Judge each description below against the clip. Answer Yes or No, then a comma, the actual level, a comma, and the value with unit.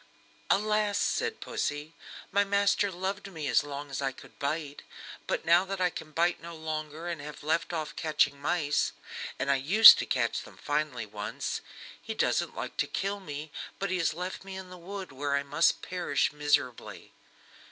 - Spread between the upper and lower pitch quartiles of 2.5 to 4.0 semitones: No, average, 4.5 semitones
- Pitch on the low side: No, medium, 160 Hz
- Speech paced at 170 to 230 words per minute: Yes, average, 185 wpm